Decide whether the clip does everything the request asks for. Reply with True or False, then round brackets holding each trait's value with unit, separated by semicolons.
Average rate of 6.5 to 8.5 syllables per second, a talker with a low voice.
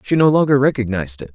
True (7.2 syllables/s; 120 Hz)